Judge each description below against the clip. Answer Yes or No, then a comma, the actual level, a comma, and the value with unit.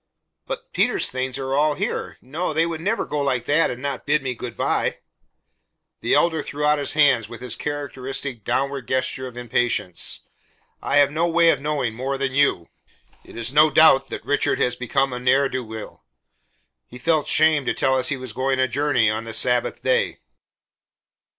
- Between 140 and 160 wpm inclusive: No, average, 190 wpm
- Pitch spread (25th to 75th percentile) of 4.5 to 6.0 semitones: No, average, 3.1 semitones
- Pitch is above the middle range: No, low, 135 Hz